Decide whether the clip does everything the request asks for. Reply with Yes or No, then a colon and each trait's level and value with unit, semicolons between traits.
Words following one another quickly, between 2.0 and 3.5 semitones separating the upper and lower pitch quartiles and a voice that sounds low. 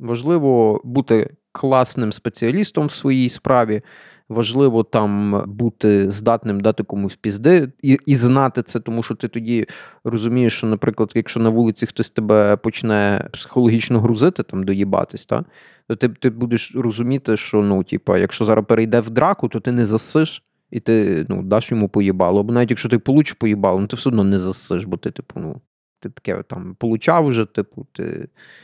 Yes: fast, 175 wpm; narrow, 2.6 semitones; low, 115 Hz